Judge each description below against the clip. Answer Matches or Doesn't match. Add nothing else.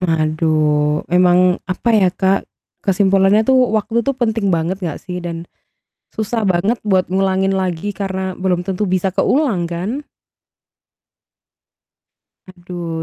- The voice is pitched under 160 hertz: Doesn't match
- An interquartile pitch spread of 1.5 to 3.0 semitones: Matches